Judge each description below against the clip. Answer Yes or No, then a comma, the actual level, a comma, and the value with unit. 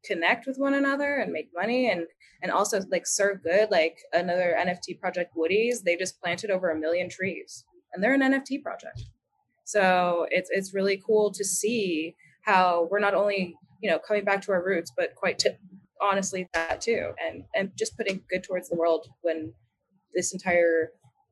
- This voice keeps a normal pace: Yes, average, 180 wpm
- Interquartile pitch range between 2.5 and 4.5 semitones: Yes, average, 3.7 semitones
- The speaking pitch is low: No, high, 190 Hz